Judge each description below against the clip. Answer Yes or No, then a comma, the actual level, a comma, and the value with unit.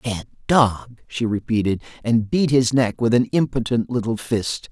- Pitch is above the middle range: No, low, 115 Hz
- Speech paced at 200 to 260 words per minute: No, average, 165 wpm